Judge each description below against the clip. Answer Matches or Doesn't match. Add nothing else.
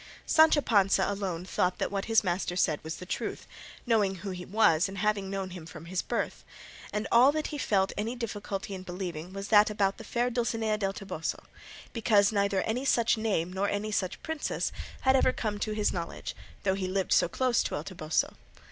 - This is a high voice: Matches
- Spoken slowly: Doesn't match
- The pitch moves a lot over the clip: Doesn't match